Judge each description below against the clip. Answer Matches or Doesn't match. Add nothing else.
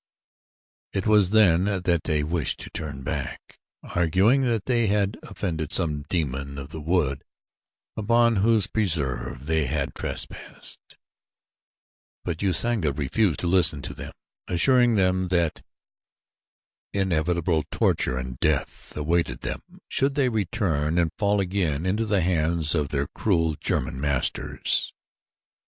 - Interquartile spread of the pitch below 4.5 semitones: Doesn't match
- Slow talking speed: Matches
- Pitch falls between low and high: Doesn't match